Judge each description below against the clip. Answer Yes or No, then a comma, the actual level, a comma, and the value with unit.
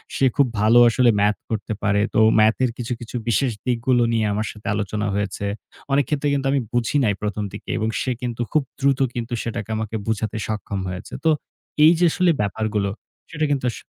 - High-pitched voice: No, low, 110 Hz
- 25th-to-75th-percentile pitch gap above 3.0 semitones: Yes, average, 3.6 semitones